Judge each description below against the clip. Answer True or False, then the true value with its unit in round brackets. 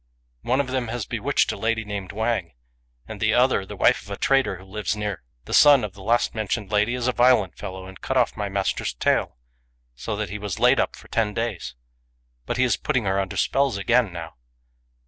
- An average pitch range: True (3.9 semitones)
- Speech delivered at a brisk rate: True (225 wpm)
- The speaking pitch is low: True (105 Hz)